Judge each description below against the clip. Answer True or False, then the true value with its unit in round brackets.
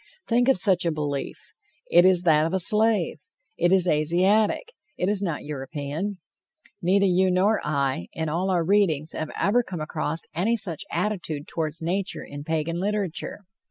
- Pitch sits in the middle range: True (175 Hz)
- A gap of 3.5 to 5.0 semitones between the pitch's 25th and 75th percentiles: True (4.3 semitones)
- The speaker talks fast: False (165 wpm)